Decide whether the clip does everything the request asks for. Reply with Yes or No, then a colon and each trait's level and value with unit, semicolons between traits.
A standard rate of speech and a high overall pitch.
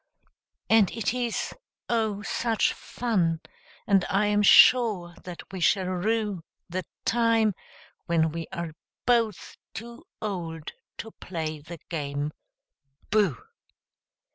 No: slow, 110 wpm; high, 195 Hz